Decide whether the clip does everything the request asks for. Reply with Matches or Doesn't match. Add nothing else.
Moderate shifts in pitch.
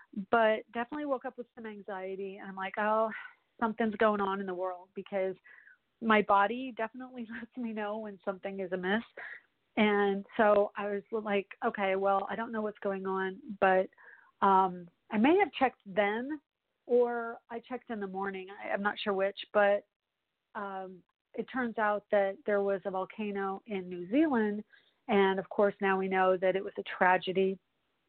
Matches